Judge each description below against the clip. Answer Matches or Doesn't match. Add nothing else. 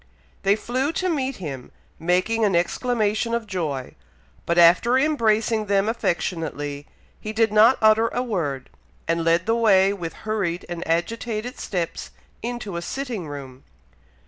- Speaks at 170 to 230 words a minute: Doesn't match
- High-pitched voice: Matches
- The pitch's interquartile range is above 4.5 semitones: Matches